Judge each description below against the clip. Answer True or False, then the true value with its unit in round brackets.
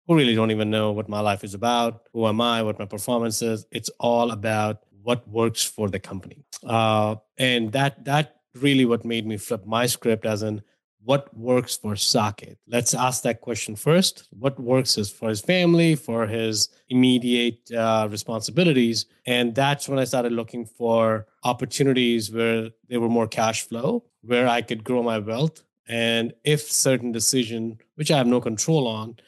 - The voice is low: True (115 Hz)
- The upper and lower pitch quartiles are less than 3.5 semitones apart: True (2.4 semitones)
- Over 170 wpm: True (180 wpm)